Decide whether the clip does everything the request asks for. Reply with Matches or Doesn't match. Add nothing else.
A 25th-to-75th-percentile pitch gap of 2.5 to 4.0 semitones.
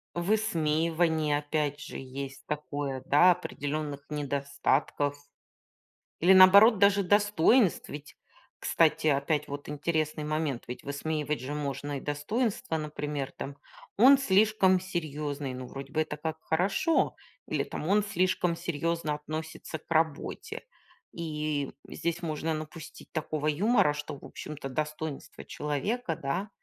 Matches